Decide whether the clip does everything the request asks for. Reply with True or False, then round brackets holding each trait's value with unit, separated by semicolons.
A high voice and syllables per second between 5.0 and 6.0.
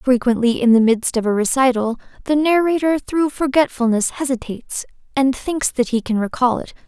True (255 Hz; 5.2 syllables/s)